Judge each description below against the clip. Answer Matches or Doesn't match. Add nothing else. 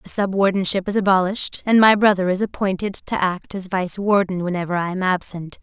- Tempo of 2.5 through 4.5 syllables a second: Doesn't match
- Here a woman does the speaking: Matches